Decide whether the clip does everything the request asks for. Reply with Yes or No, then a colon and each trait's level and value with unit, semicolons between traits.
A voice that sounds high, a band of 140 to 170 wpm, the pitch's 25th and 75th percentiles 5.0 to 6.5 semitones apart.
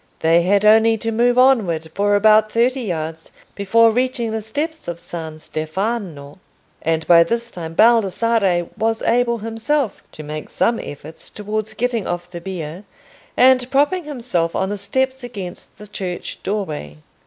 Yes: high, 210 Hz; average, 155 wpm; wide, 5.5 semitones